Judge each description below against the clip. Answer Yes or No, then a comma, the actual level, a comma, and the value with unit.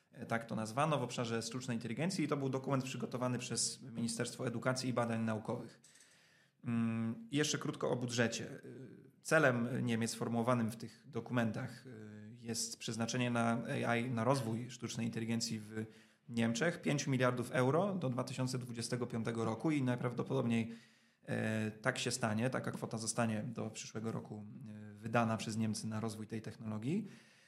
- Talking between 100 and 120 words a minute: No, average, 135 wpm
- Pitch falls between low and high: No, low, 115 Hz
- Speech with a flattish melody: Yes, narrow, 2.1 semitones